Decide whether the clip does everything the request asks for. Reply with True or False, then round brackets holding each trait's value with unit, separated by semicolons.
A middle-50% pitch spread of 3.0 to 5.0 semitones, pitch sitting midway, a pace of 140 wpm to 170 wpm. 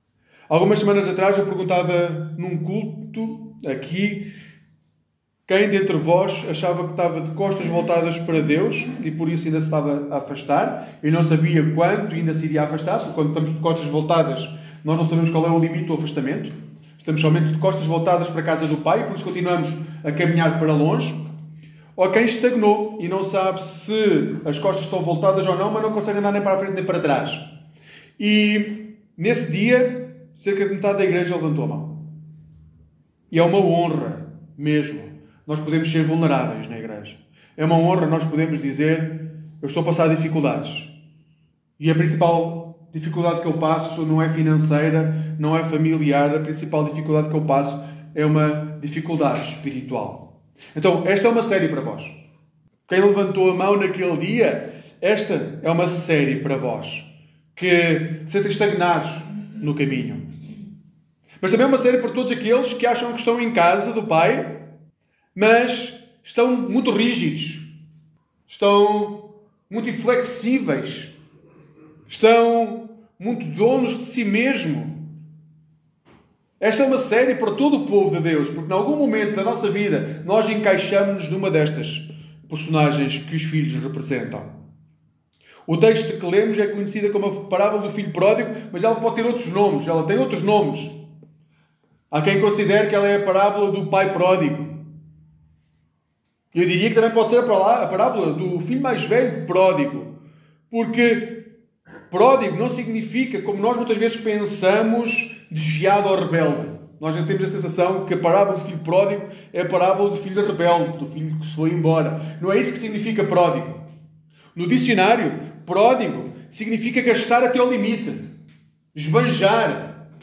True (4.7 semitones; 170 Hz; 160 wpm)